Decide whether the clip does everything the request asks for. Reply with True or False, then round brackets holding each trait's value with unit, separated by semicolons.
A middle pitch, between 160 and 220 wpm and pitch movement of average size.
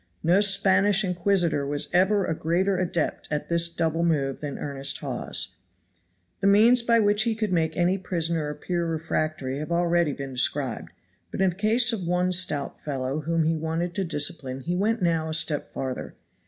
True (170 Hz; 180 wpm; 4.1 semitones)